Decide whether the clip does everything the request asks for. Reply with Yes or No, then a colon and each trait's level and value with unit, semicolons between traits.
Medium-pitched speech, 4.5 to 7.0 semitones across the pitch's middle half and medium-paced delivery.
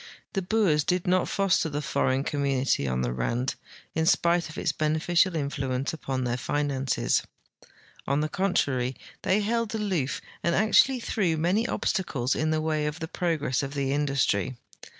Yes: medium, 150 Hz; average, 4.8 semitones; average, 165 wpm